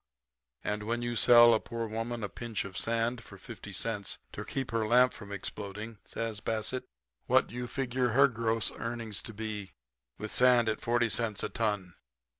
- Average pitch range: No, narrow, 2.1 semitones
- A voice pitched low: Yes, low, 115 Hz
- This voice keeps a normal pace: Yes, average, 185 wpm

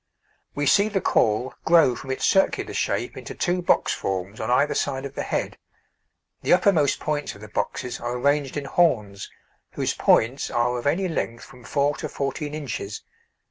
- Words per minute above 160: Yes, average, 180 wpm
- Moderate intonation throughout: Yes, average, 4.2 semitones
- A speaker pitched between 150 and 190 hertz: No, medium, 140 Hz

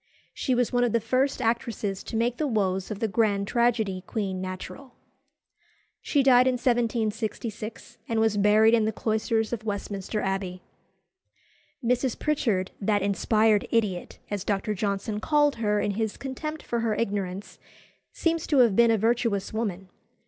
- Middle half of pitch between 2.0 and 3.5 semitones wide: Yes, average, 2.9 semitones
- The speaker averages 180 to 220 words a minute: No, average, 155 wpm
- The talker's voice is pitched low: No, high, 220 Hz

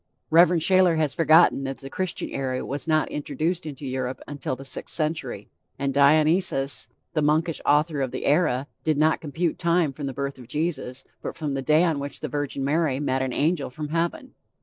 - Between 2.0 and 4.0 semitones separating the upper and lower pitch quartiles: Yes, average, 2.9 semitones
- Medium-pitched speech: Yes, medium, 150 Hz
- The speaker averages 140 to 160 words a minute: No, average, 195 wpm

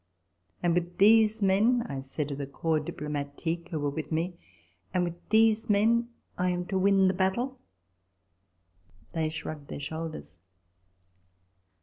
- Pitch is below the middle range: No, medium, 175 Hz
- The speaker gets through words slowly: No, average, 150 wpm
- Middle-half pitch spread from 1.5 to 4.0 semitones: No, average, 5.1 semitones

